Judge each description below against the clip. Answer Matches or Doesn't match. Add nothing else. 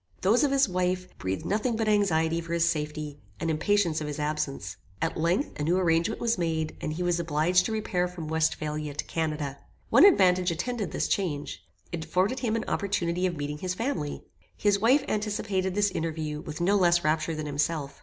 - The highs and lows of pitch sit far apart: Doesn't match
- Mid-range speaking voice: Matches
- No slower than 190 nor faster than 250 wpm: Matches